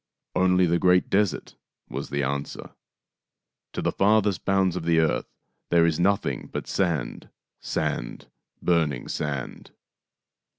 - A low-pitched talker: Yes, very low, 85 Hz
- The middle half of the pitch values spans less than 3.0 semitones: No, average, 3.7 semitones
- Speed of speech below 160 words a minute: Yes, slow, 135 wpm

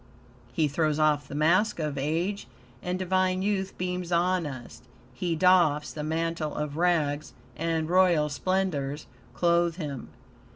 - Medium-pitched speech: Yes, medium, 165 Hz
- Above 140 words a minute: No, slow, 135 wpm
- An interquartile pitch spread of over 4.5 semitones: No, average, 3.3 semitones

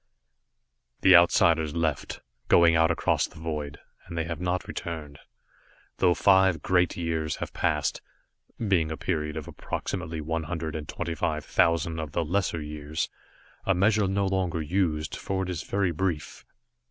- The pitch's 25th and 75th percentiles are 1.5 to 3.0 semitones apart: Yes, narrow, 2.6 semitones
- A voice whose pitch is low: Yes, very low, 85 Hz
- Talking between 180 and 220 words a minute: No, average, 155 wpm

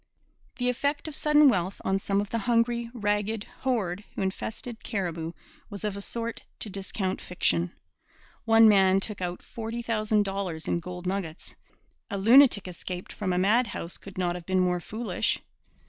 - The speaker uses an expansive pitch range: No, average, 3.9 semitones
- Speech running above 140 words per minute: Yes, average, 165 wpm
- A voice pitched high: Yes, high, 200 Hz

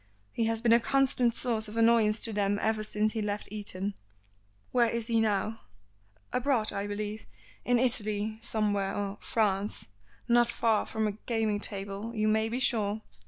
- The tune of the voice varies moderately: No, narrow, 1.9 semitones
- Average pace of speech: Yes, average, 165 wpm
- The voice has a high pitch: Yes, high, 220 Hz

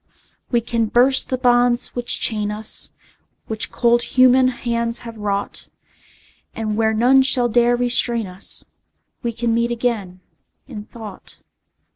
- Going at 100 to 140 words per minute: Yes, slow, 135 wpm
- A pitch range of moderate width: No, narrow, 1.9 semitones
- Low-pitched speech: No, high, 235 Hz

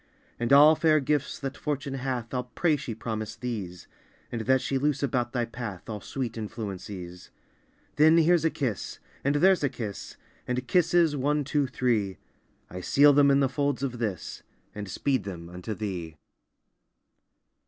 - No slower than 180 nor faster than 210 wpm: No, average, 165 wpm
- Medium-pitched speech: No, low, 125 Hz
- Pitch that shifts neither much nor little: Yes, average, 4.9 semitones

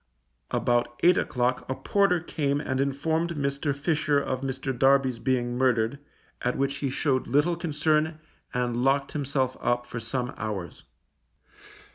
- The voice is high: No, low, 135 Hz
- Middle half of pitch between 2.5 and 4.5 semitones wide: Yes, average, 2.9 semitones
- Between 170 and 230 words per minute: No, slow, 135 wpm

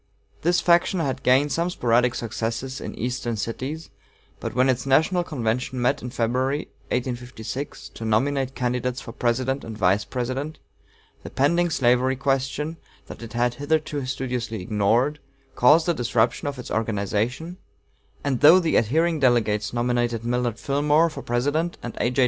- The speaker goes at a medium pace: Yes, average, 150 wpm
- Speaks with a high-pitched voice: No, low, 125 Hz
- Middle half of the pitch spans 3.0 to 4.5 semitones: Yes, average, 3.4 semitones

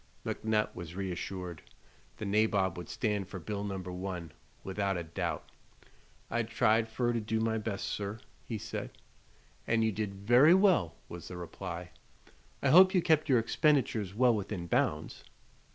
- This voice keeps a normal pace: Yes, average, 155 wpm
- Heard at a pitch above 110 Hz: No, low, 105 Hz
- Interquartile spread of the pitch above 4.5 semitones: No, average, 3.7 semitones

